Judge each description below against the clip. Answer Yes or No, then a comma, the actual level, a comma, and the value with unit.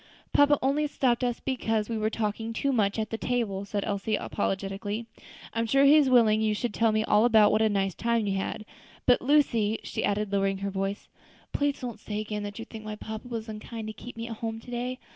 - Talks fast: Yes, fast, 230 wpm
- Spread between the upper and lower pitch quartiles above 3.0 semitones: No, narrow, 2.6 semitones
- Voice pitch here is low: No, high, 220 Hz